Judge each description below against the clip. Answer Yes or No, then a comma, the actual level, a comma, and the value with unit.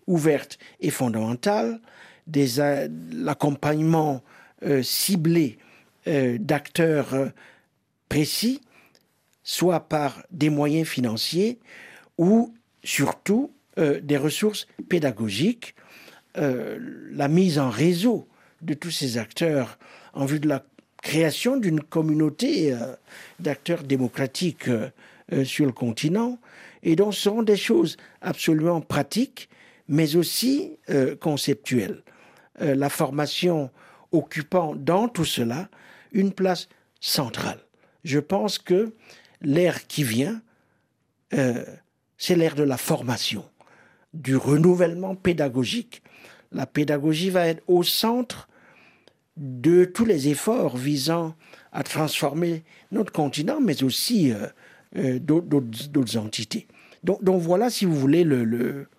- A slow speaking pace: Yes, slow, 115 wpm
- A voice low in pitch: No, medium, 155 Hz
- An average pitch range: Yes, average, 4.6 semitones